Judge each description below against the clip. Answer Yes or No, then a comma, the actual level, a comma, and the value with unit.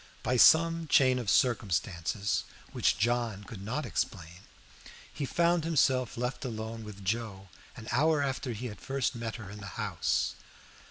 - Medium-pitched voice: No, low, 120 Hz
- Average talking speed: Yes, average, 155 wpm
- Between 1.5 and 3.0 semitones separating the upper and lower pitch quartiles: No, average, 4.3 semitones